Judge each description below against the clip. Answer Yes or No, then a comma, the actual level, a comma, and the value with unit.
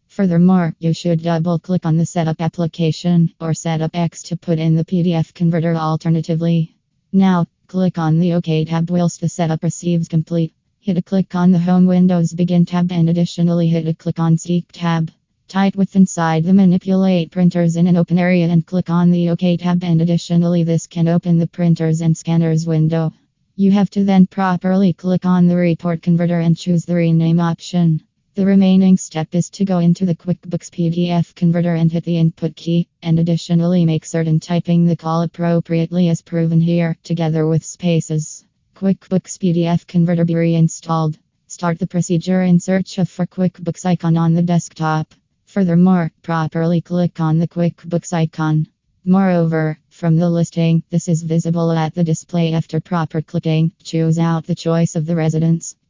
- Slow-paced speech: No, average, 175 wpm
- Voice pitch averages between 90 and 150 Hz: No, medium, 170 Hz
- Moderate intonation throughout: No, narrow, 1.3 semitones